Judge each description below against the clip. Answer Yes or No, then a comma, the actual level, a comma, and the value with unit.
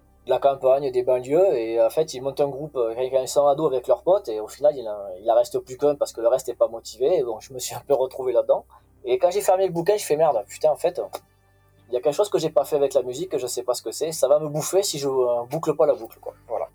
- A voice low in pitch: No, medium, 150 Hz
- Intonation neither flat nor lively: No, wide, 8.2 semitones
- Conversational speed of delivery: No, fast, 305 wpm